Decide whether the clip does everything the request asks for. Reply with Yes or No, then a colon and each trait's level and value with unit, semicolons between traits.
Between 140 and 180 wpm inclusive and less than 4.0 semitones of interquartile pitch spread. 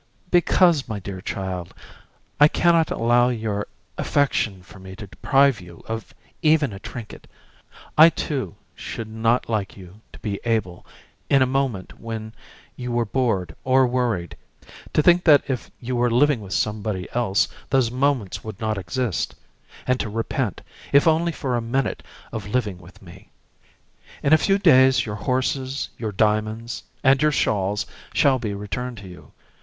No: average, 160 wpm; average, 4.5 semitones